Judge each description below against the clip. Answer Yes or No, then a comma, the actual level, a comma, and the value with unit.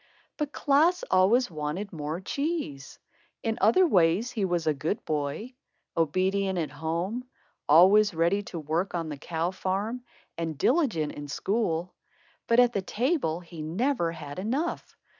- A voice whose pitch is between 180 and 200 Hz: Yes, medium, 185 Hz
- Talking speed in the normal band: Yes, average, 145 wpm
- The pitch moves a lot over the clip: Yes, wide, 6.3 semitones